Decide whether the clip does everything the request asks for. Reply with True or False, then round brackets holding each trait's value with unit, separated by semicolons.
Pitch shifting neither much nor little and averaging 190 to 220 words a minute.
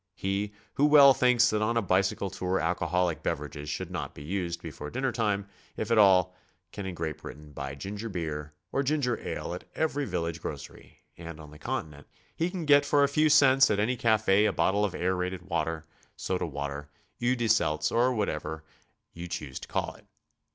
False (6.5 semitones; 195 wpm)